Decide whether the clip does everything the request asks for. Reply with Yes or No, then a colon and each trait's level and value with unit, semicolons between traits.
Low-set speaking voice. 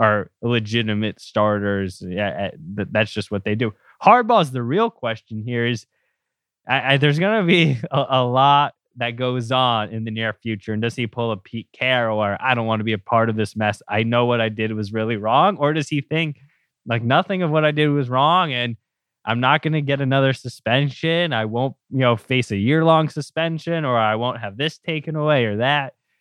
Yes: low, 120 Hz